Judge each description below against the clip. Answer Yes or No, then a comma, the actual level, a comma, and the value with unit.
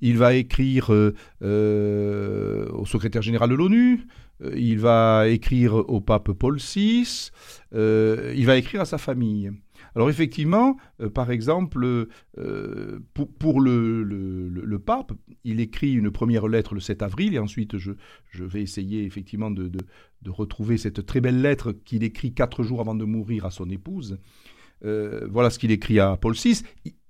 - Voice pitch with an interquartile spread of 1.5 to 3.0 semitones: No, average, 3.5 semitones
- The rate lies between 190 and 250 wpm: No, average, 175 wpm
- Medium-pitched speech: No, low, 115 Hz